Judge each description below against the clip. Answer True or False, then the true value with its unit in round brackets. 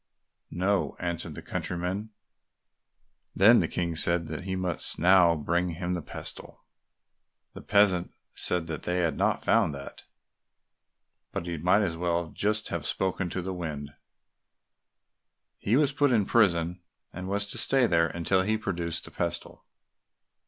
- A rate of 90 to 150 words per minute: True (145 wpm)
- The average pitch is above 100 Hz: False (90 Hz)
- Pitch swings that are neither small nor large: False (2.3 semitones)